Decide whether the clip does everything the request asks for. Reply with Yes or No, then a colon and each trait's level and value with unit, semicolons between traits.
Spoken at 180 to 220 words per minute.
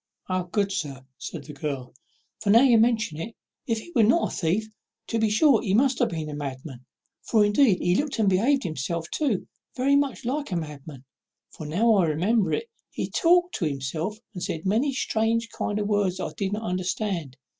Yes: average, 200 wpm